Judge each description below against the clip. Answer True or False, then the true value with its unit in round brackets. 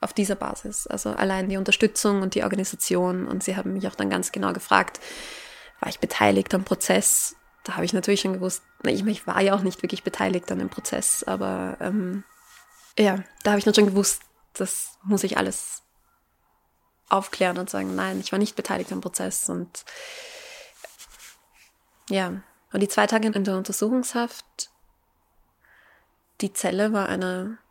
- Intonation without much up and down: True (2.3 semitones)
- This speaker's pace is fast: False (170 wpm)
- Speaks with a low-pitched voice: False (195 Hz)